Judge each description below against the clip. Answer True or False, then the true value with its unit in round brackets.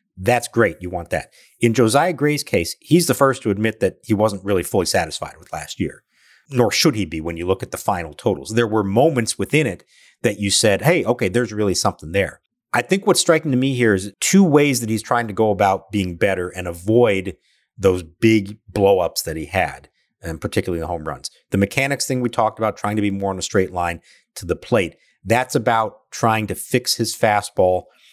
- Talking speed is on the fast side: True (220 wpm)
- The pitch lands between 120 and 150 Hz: False (110 Hz)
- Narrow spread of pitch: False (4.3 semitones)